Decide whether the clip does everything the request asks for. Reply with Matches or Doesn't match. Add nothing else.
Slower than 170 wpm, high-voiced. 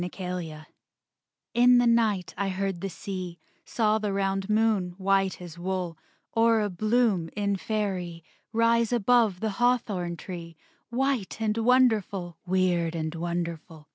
Matches